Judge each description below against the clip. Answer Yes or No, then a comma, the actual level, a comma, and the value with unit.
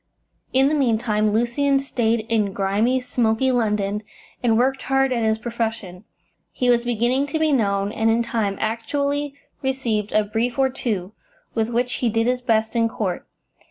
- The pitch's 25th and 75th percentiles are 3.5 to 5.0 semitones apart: No, average, 2.8 semitones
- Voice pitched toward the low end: No, high, 230 Hz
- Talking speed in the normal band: Yes, average, 165 wpm